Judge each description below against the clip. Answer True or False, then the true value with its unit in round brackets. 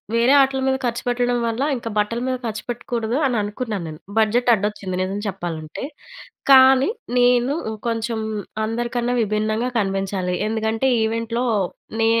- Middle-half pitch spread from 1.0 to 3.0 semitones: True (2.7 semitones)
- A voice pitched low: False (230 Hz)